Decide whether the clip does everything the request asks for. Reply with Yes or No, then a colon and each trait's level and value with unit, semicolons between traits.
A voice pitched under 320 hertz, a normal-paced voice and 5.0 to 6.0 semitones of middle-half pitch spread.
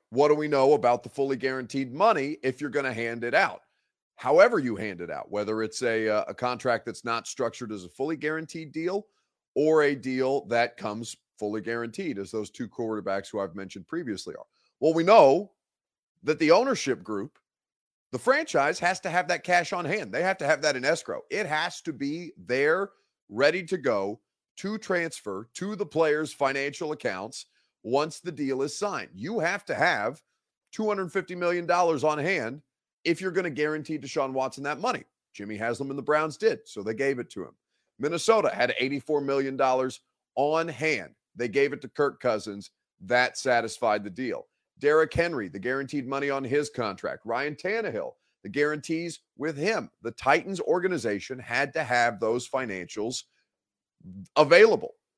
Yes: medium, 140 Hz; average, 175 wpm; wide, 5.6 semitones